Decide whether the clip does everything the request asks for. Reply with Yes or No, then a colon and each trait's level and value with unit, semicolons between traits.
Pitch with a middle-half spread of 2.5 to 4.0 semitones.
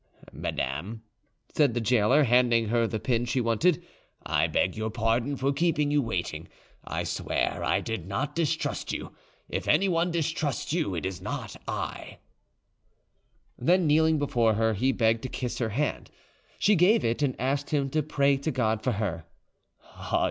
No: average, 4.9 semitones